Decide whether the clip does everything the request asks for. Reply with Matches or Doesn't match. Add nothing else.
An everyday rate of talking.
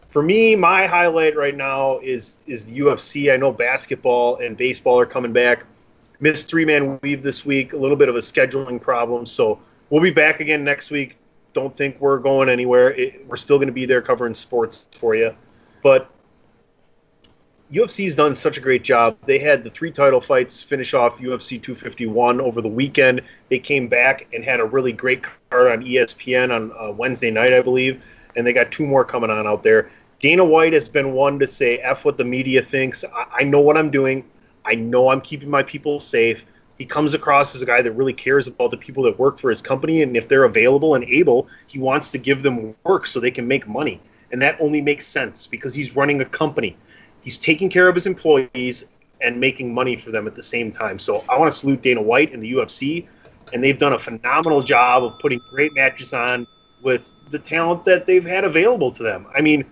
Doesn't match